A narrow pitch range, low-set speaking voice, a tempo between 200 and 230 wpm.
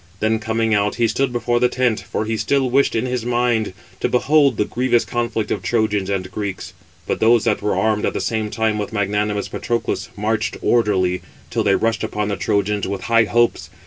Yes: narrow, 2.3 semitones; low, 110 Hz; fast, 205 wpm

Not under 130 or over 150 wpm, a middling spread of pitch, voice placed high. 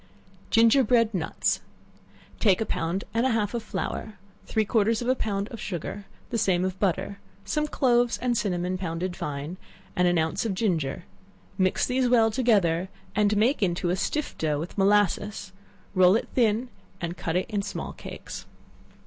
No: average, 175 wpm; average, 4.2 semitones; high, 205 Hz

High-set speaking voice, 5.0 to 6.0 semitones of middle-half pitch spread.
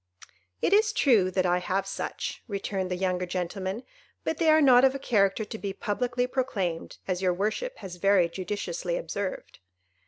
Yes: high, 195 Hz; average, 5.3 semitones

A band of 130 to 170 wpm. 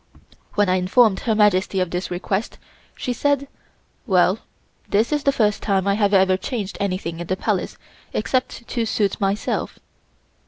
Yes: average, 160 wpm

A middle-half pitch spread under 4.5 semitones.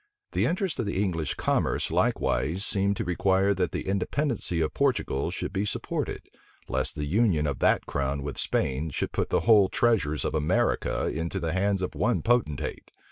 No: average, 5.1 semitones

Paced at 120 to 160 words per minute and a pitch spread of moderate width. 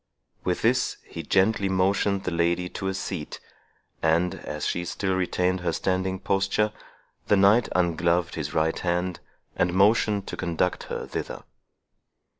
No: average, 145 wpm; narrow, 2.1 semitones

